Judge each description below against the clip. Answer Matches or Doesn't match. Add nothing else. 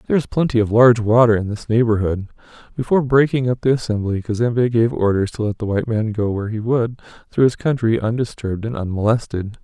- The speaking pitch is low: Matches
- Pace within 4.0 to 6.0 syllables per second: Doesn't match